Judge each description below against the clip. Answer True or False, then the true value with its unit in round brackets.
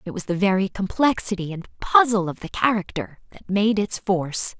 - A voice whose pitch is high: True (195 Hz)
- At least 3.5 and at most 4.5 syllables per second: False (5.2 syllables/s)